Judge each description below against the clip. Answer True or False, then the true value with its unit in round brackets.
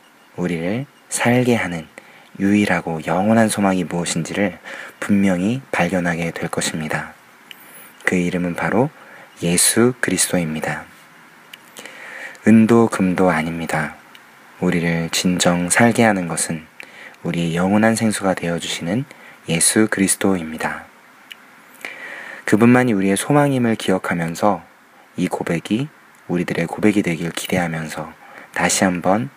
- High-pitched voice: False (95 Hz)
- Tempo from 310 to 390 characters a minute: False (265 characters per minute)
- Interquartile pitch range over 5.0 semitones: False (4.3 semitones)